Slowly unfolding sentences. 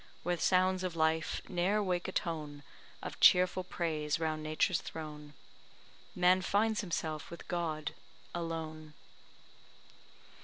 Yes: slow, 115 wpm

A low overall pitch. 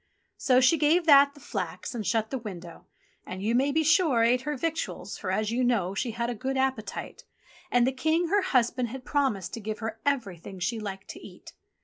No: high, 245 Hz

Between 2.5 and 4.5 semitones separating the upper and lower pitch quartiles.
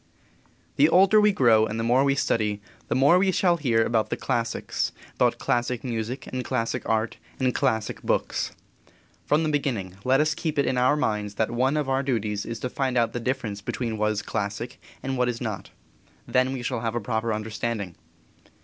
Yes: average, 3.3 semitones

